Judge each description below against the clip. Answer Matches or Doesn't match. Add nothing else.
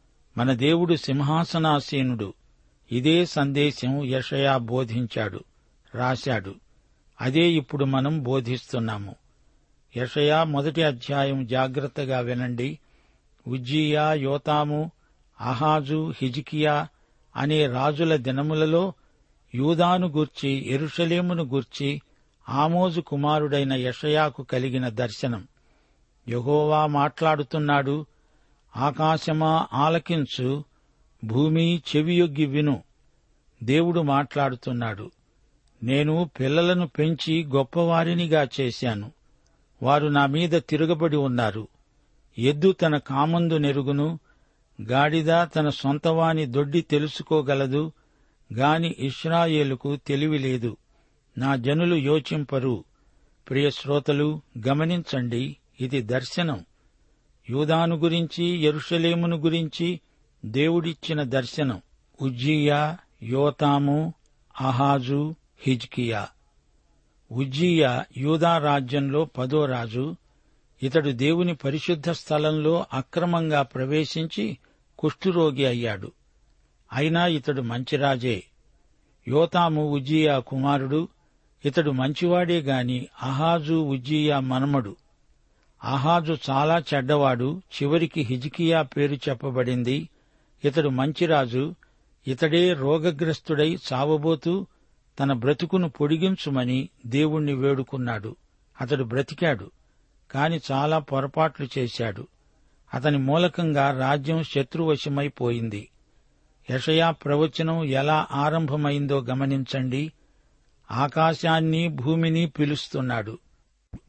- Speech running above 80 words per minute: Doesn't match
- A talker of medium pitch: Matches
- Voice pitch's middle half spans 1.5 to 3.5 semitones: Matches